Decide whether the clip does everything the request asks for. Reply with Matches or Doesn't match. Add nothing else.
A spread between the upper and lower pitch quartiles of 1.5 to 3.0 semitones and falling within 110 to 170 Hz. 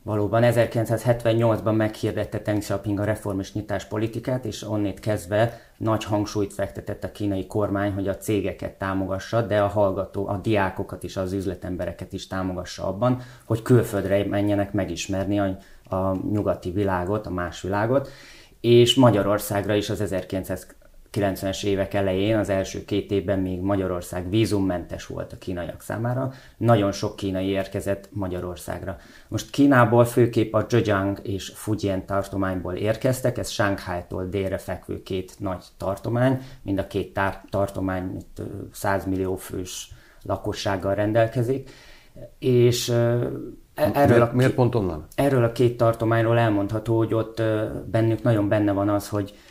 Doesn't match